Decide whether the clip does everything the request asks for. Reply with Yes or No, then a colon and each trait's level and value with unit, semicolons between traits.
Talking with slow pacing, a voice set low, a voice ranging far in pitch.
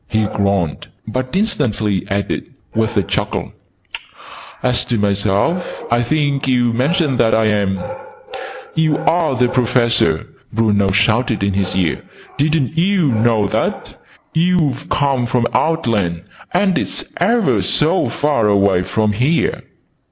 Yes: slow, 130 wpm; low, 120 Hz; wide, 6.6 semitones